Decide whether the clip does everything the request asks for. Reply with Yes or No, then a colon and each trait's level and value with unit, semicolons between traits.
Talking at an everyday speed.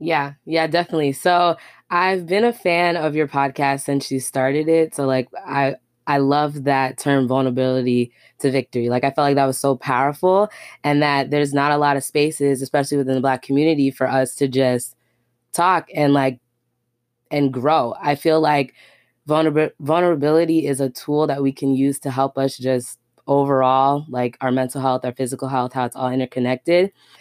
Yes: average, 185 wpm